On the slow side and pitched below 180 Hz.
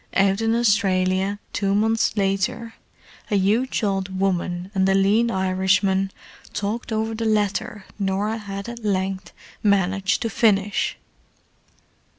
No: slow, 125 wpm; high, 200 Hz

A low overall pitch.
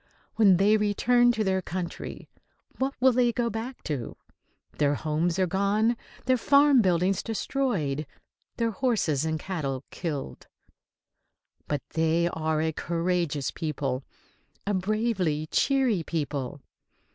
No: medium, 185 Hz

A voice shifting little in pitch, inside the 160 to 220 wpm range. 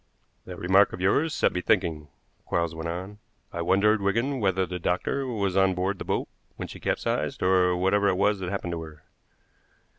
Yes: narrow, 2.3 semitones; average, 190 wpm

